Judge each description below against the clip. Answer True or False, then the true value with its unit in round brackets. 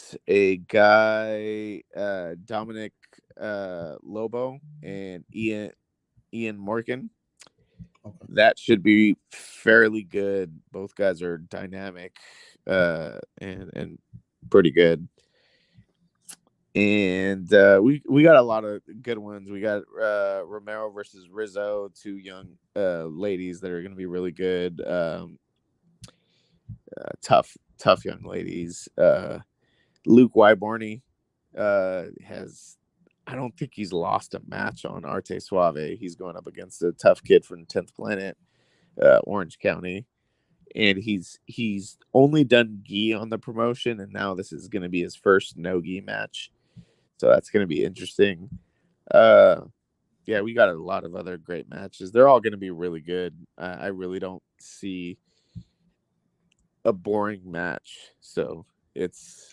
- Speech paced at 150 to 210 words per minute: False (140 wpm)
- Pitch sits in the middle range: False (100 Hz)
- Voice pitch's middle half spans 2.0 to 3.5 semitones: True (3.0 semitones)